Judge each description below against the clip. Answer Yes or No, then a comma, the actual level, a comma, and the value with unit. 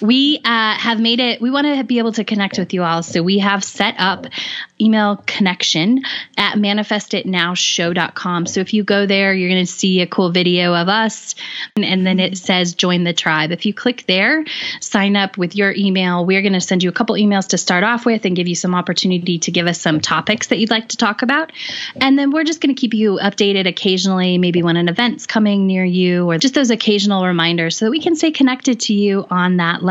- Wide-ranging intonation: No, average, 4.0 semitones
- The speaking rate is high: Yes, fast, 235 wpm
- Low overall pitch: No, high, 200 Hz